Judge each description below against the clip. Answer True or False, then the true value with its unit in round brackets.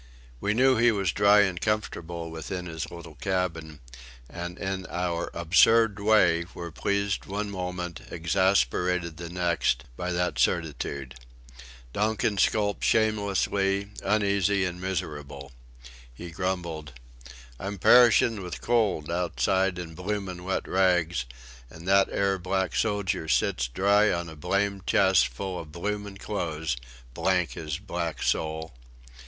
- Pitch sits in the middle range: False (90 Hz)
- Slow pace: True (125 wpm)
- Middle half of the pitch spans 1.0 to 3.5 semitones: True (3.2 semitones)